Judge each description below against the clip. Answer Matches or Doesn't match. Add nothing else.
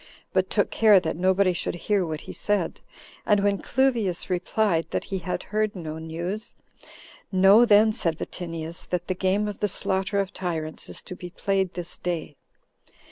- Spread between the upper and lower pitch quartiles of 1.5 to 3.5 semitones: Matches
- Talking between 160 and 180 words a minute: Matches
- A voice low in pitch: Doesn't match